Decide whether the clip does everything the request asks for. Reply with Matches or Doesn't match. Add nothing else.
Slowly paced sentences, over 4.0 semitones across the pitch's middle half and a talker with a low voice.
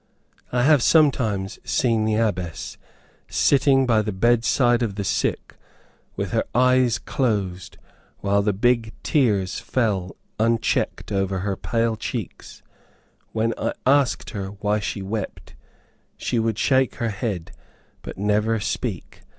Doesn't match